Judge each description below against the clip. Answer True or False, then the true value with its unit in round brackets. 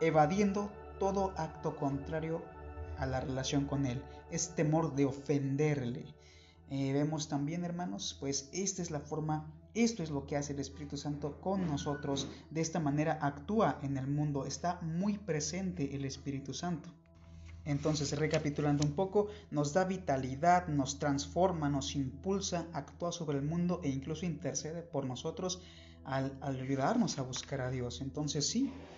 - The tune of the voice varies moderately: True (3.5 semitones)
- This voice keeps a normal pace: True (155 wpm)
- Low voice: False (145 Hz)